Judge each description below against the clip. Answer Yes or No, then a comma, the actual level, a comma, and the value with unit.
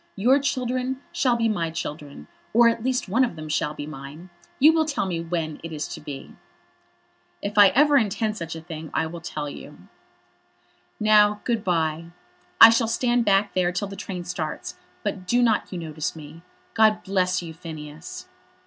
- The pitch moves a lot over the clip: Yes, wide, 6.0 semitones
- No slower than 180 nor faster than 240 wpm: Yes, average, 185 wpm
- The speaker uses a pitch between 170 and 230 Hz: Yes, medium, 185 Hz